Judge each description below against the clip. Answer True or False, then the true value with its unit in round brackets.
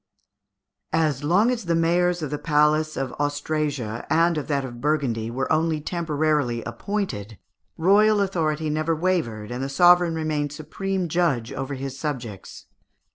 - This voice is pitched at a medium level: True (155 Hz)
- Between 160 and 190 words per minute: False (145 wpm)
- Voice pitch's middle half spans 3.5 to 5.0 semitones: True (3.9 semitones)